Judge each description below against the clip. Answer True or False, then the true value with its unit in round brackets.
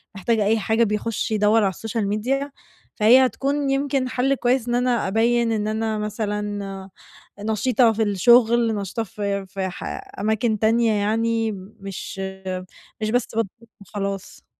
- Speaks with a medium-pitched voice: False (220 Hz)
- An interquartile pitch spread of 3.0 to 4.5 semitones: False (2.5 semitones)